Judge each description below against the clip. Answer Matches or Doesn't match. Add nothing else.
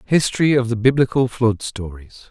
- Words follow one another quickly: Doesn't match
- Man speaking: Matches